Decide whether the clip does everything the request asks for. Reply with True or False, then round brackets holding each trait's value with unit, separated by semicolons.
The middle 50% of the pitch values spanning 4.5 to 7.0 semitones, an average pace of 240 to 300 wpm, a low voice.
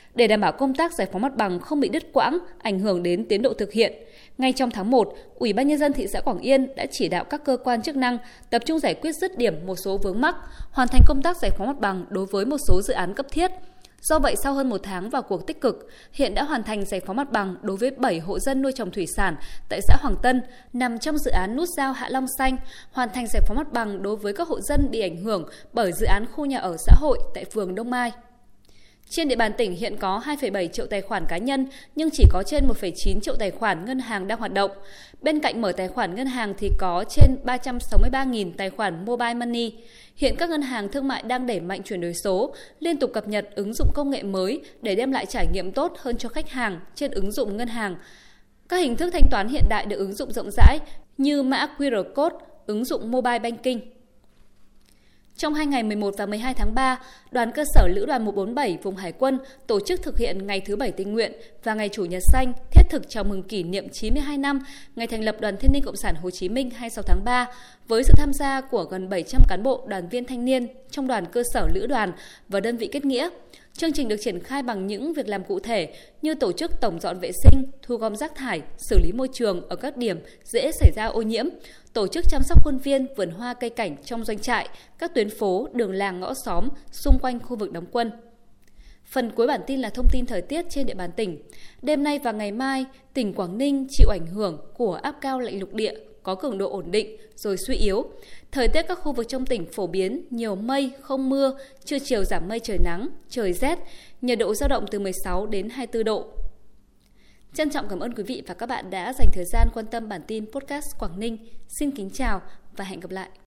False (5.2 semitones; 245 wpm; 240 Hz)